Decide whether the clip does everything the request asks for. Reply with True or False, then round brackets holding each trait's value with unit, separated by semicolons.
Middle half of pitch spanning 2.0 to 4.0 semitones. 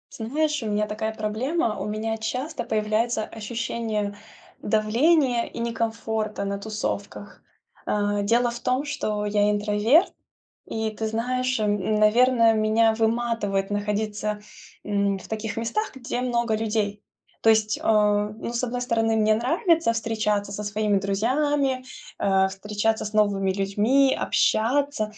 True (2.4 semitones)